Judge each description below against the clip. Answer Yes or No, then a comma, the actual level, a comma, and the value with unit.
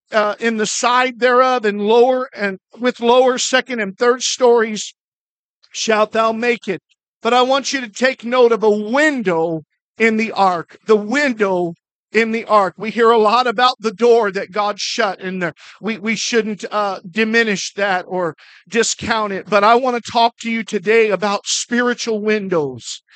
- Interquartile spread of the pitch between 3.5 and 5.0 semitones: No, average, 2.8 semitones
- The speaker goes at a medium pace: Yes, average, 175 wpm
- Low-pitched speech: No, high, 225 Hz